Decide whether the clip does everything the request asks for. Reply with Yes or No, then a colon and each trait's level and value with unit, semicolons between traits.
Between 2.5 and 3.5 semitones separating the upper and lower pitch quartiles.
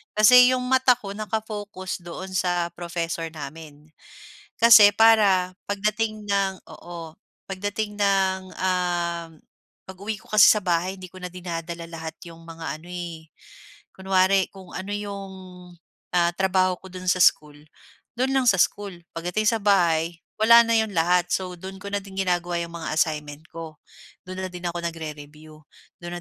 Yes: average, 3.1 semitones